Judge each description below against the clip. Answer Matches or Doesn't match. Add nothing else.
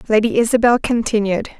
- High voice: Matches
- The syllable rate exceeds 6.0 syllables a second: Matches